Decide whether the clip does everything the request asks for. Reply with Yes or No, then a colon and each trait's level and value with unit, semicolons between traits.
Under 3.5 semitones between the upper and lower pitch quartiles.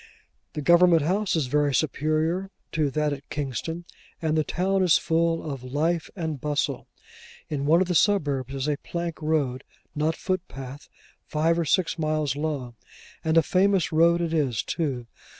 Yes: average, 2.8 semitones